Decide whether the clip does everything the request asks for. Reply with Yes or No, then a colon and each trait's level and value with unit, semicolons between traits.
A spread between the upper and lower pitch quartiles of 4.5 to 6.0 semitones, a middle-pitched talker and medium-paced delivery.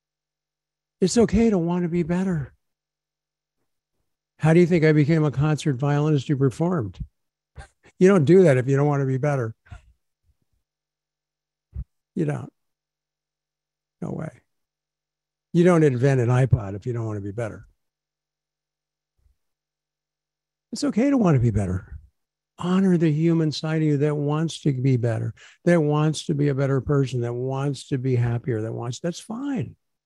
Yes: average, 4.8 semitones; medium, 150 Hz; average, 160 wpm